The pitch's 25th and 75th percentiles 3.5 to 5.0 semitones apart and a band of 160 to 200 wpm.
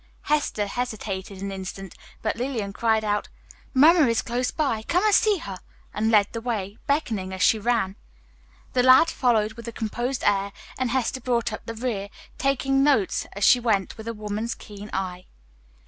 Yes: average, 3.9 semitones; average, 180 wpm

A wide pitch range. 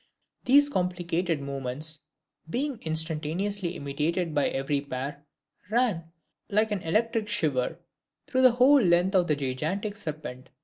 Yes: wide, 6.0 semitones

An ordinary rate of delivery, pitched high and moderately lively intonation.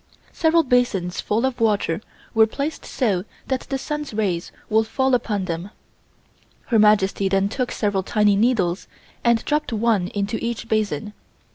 Yes: average, 150 wpm; high, 220 Hz; average, 3.9 semitones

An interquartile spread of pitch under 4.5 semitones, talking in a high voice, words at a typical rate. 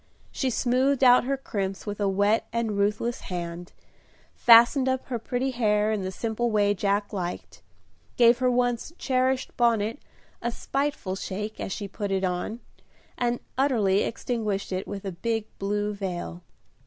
Yes: average, 3.6 semitones; high, 215 Hz; average, 155 wpm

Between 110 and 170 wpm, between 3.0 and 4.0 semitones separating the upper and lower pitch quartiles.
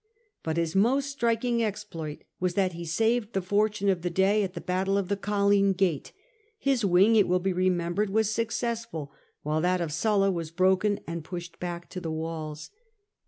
No: average, 190 wpm; average, 3.5 semitones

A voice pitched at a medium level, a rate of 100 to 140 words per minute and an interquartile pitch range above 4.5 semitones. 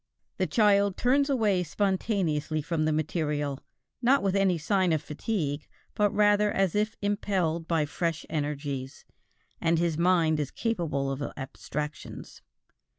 Yes: medium, 170 Hz; slow, 135 wpm; average, 5.2 semitones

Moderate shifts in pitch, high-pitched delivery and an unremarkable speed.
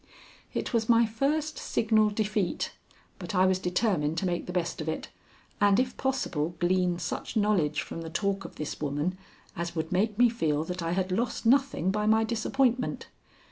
Yes: average, 4.7 semitones; high, 195 Hz; average, 180 wpm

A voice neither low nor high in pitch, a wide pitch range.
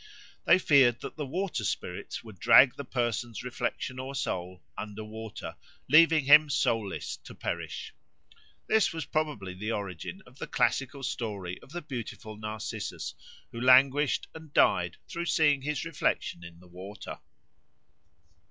No: low, 125 Hz; wide, 5.8 semitones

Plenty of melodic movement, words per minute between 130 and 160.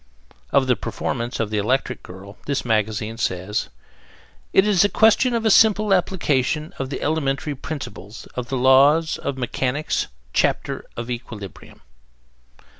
Yes: wide, 5.7 semitones; average, 140 wpm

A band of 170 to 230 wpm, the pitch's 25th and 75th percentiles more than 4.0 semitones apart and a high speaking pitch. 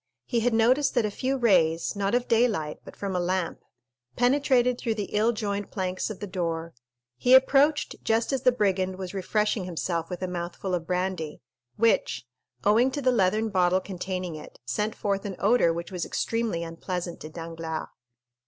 Yes: average, 180 wpm; average, 4.6 semitones; high, 195 Hz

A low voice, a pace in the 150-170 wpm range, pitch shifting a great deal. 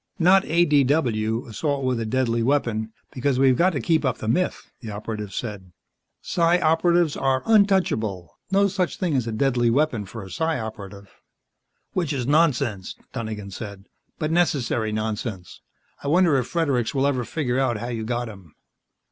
Yes: low, 125 Hz; average, 165 wpm; wide, 6.2 semitones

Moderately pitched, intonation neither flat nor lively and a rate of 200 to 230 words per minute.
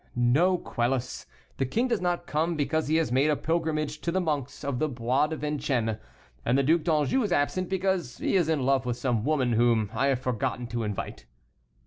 Yes: medium, 145 Hz; average, 4.7 semitones; fast, 205 wpm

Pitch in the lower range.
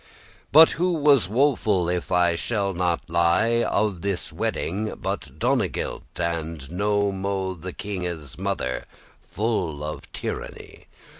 Yes: very low, 95 Hz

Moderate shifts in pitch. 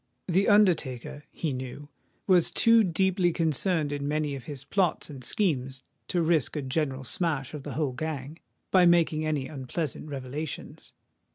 Yes: average, 4.2 semitones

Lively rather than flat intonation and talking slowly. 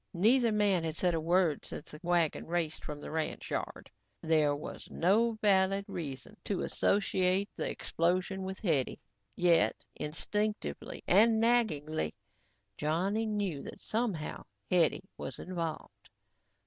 No: average, 4.4 semitones; slow, 130 wpm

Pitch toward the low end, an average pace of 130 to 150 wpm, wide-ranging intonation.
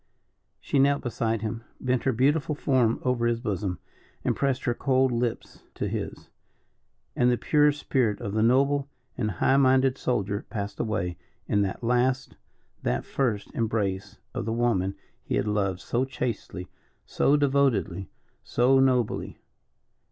No: low, 120 Hz; average, 145 wpm; average, 4.0 semitones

